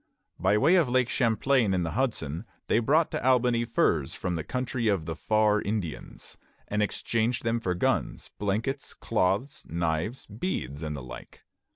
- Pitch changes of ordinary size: No, wide, 6.1 semitones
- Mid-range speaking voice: No, low, 110 Hz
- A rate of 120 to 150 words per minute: No, average, 165 wpm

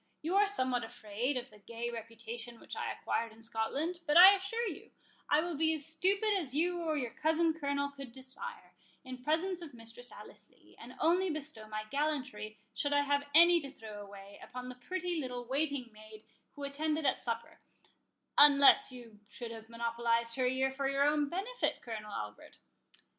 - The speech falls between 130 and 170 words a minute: No, average, 180 wpm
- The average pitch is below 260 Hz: No, very high, 275 Hz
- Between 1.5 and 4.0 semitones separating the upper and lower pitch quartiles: No, average, 5.3 semitones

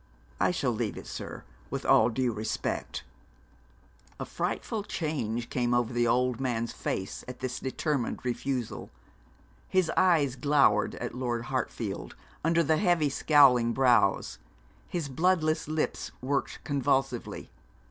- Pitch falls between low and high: No, low, 130 Hz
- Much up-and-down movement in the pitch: No, average, 4.3 semitones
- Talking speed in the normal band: No, slow, 125 wpm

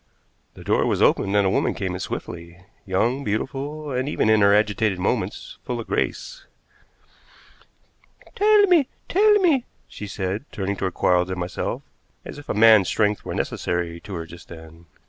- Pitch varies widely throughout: Yes, wide, 6.9 semitones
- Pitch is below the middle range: Yes, low, 105 Hz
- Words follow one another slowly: No, average, 170 wpm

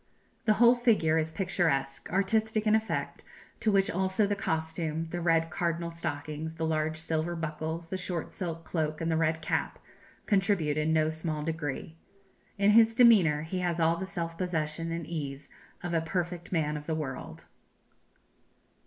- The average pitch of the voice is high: No, medium, 165 Hz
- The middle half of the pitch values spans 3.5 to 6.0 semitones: No, average, 2.9 semitones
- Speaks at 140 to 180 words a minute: Yes, average, 165 wpm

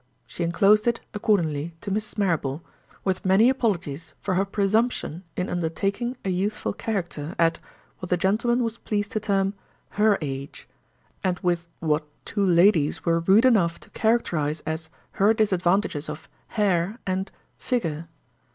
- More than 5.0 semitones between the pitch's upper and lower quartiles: No, average, 4.1 semitones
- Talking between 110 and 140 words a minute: Yes, slow, 135 wpm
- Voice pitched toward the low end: No, high, 190 Hz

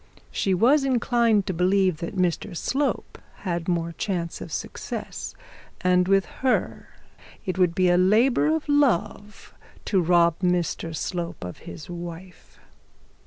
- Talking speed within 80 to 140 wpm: Yes, slow, 135 wpm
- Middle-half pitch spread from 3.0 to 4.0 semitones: Yes, average, 3.7 semitones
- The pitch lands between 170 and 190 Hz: Yes, medium, 185 Hz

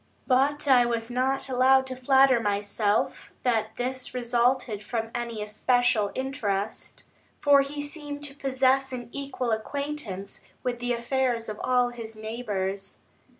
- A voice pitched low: No, high, 245 Hz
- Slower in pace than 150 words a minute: Yes, slow, 135 wpm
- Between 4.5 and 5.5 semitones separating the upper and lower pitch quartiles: No, average, 3.1 semitones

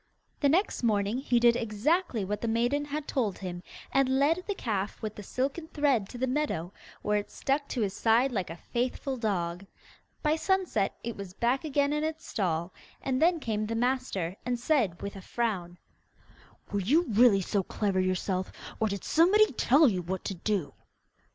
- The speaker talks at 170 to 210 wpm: Yes, average, 185 wpm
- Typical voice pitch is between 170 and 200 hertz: No, high, 235 Hz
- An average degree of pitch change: No, wide, 6.2 semitones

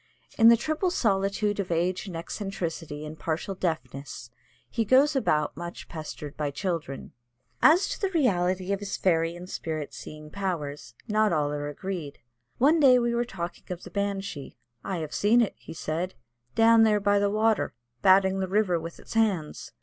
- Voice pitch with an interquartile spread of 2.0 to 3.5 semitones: No, average, 5.0 semitones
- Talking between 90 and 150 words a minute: No, average, 175 wpm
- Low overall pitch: No, medium, 185 Hz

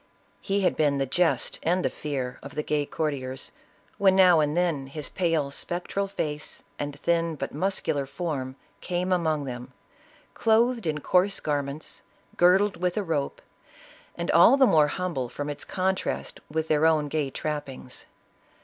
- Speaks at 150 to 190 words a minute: Yes, average, 160 wpm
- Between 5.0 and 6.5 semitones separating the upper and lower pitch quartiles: No, average, 4.0 semitones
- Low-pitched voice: No, medium, 155 Hz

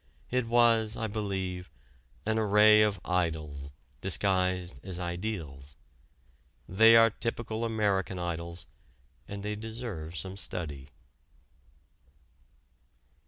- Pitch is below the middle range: Yes, very low, 95 Hz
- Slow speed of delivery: Yes, slow, 95 wpm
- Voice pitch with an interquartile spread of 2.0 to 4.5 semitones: Yes, average, 4.0 semitones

